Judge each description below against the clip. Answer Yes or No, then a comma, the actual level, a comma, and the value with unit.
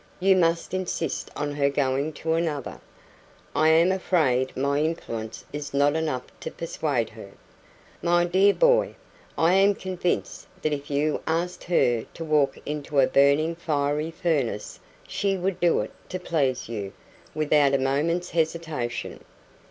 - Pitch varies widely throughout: No, average, 3.5 semitones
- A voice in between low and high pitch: Yes, medium, 155 Hz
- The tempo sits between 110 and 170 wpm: Yes, average, 145 wpm